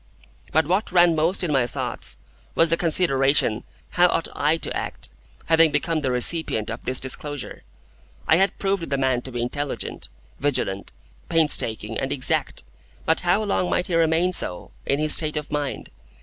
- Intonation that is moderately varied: Yes, average, 4.1 semitones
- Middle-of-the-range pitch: Yes, medium, 150 Hz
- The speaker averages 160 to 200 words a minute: Yes, average, 170 wpm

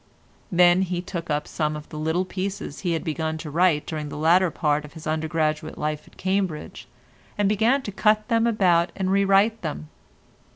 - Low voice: No, medium, 175 Hz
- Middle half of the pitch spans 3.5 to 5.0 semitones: Yes, average, 3.9 semitones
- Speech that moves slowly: No, average, 195 wpm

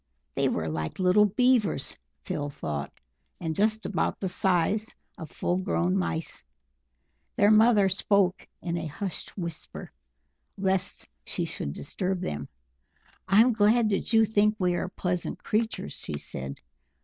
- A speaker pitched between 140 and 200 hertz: Yes, high, 190 Hz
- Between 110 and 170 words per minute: Yes, slow, 135 wpm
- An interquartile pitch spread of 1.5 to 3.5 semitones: No, average, 4.2 semitones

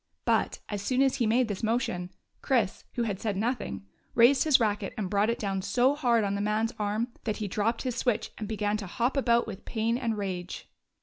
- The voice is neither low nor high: No, high, 220 Hz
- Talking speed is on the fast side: Yes, fast, 220 wpm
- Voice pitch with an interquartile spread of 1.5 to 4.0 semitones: Yes, average, 2.8 semitones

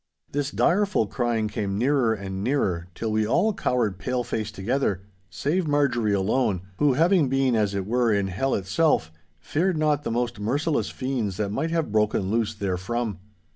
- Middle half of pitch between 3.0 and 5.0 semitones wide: No, wide, 5.6 semitones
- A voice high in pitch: No, low, 115 Hz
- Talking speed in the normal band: Yes, average, 160 wpm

